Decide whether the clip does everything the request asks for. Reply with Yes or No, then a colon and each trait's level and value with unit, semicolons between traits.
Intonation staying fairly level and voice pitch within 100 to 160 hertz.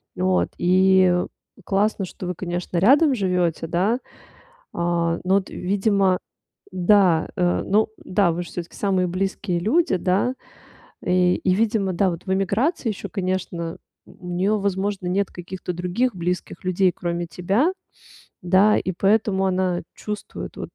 No: narrow, 2.1 semitones; medium, 185 Hz